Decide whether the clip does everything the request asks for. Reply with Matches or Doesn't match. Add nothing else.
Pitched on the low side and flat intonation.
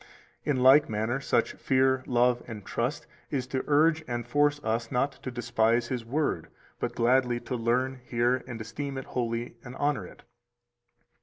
Matches